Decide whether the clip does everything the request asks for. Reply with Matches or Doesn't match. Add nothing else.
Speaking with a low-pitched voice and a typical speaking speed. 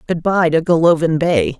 Doesn't match